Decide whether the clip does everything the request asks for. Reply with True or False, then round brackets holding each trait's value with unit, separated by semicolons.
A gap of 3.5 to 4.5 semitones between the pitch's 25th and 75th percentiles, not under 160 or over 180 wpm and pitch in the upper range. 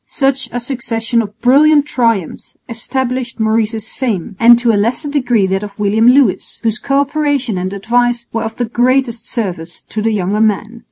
False (3.0 semitones; 175 wpm; 230 Hz)